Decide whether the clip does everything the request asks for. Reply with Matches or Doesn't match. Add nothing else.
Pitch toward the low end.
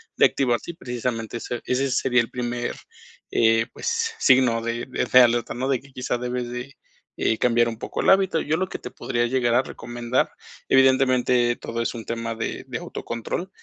Matches